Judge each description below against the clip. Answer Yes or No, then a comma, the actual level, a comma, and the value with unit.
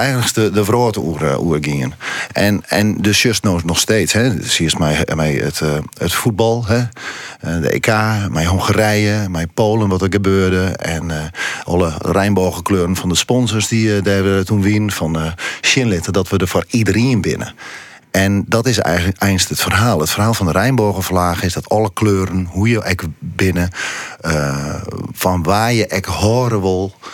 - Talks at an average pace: Yes, average, 180 wpm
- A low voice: Yes, very low, 95 Hz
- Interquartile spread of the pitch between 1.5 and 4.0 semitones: Yes, average, 3.6 semitones